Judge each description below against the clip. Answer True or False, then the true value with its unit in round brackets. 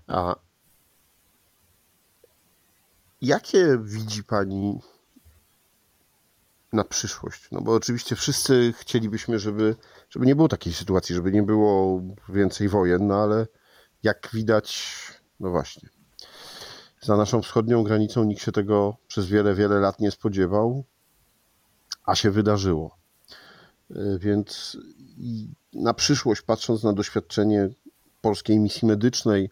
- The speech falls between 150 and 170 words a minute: False (110 wpm)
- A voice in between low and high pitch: False (105 Hz)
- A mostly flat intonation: True (2.1 semitones)